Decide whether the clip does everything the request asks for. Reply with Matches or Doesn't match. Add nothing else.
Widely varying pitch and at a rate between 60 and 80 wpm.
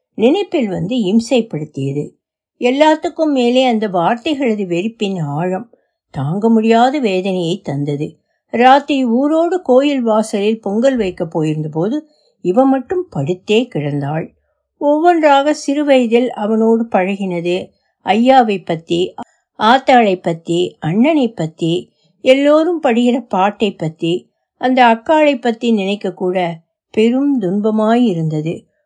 Matches